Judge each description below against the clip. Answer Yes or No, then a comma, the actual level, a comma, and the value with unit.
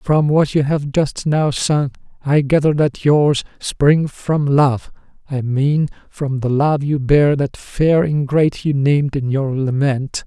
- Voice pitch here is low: No, medium, 145 Hz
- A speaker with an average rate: Yes, average, 170 wpm